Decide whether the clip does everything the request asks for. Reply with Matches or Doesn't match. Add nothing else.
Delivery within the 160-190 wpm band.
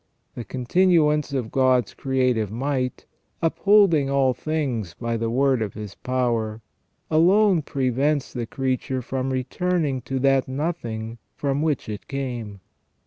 Doesn't match